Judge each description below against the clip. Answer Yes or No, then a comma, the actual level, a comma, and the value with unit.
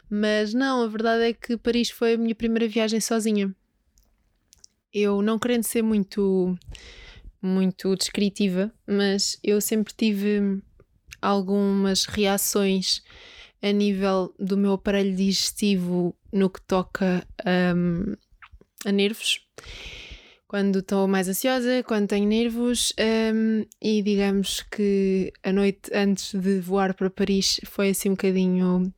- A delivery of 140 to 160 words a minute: No, average, 125 wpm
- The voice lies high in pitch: Yes, high, 200 Hz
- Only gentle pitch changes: Yes, narrow, 2.3 semitones